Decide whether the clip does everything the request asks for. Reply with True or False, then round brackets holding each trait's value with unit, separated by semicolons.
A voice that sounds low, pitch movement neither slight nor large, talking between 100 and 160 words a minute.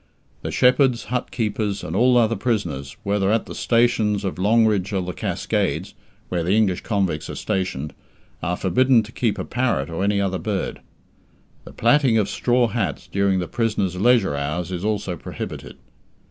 False (100 Hz; 4.0 semitones; 170 wpm)